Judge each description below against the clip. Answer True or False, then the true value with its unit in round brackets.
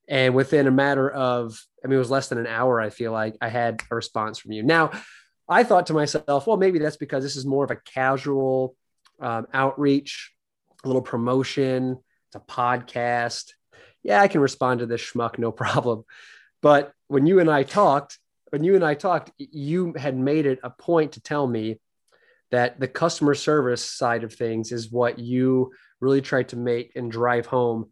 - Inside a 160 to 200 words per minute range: True (195 wpm)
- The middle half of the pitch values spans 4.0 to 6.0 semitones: False (3.1 semitones)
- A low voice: True (130 Hz)